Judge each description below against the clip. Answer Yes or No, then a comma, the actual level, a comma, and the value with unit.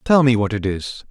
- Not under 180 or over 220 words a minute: No, fast, 270 wpm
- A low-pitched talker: Yes, low, 115 Hz